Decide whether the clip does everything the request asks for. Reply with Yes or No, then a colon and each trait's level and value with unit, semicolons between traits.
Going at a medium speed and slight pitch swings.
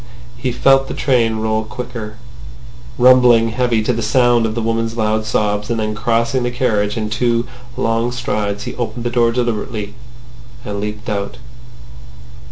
Yes: average, 160 wpm; narrow, 2.1 semitones